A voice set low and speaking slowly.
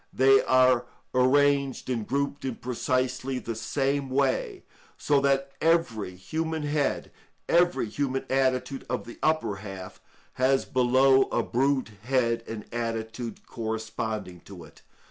Yes: low, 130 Hz; slow, 125 wpm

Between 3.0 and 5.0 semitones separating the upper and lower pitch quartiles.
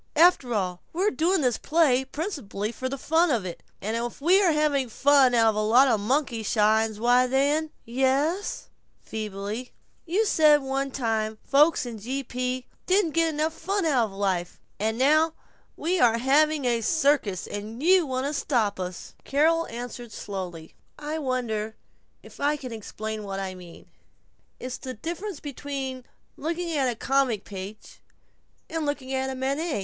No: wide, 5.5 semitones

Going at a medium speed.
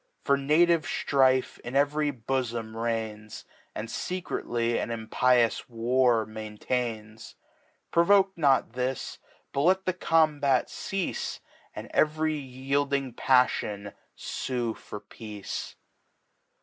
No: slow, 100 wpm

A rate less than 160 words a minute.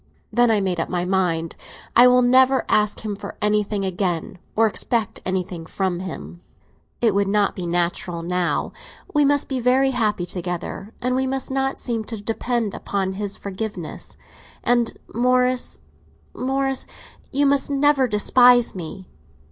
Yes: average, 150 wpm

